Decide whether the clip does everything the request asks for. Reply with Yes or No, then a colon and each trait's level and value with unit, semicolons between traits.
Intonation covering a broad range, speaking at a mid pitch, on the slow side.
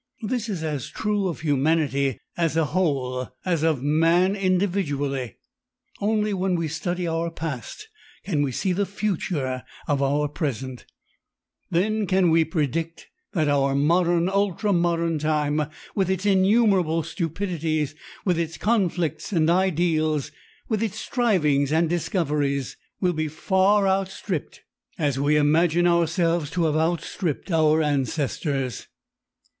No: average, 3.9 semitones; medium, 165 Hz; slow, 130 wpm